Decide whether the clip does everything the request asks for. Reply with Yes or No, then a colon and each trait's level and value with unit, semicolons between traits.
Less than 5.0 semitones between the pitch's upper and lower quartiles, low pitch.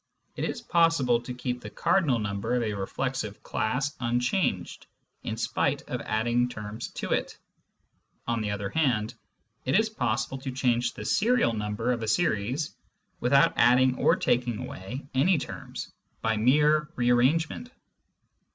Yes: average, 3.7 semitones; low, 125 Hz